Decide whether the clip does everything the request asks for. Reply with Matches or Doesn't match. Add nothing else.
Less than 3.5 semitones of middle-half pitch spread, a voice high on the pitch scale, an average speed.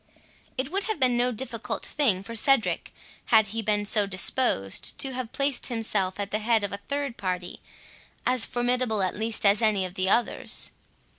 Doesn't match